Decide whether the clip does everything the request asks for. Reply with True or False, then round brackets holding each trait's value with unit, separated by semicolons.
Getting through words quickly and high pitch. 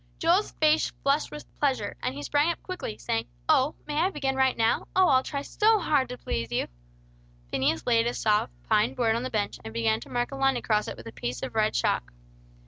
True (220 wpm; 250 Hz)